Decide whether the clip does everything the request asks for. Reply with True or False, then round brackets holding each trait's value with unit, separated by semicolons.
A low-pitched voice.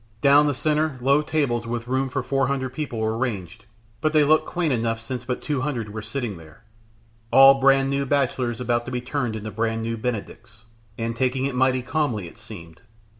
True (125 Hz)